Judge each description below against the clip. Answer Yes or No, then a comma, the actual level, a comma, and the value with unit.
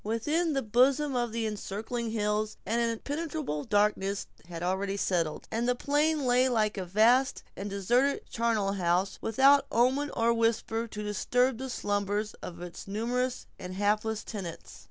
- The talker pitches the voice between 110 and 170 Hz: No, high, 225 Hz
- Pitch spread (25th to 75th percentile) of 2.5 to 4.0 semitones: Yes, average, 3.7 semitones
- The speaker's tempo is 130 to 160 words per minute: Yes, average, 155 wpm